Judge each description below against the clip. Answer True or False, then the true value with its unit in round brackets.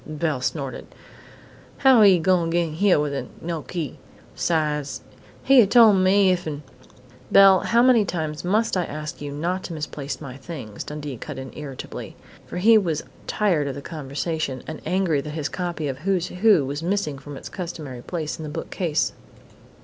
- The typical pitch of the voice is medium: True (160 Hz)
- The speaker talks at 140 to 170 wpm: False (180 wpm)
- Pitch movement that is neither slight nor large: True (4.3 semitones)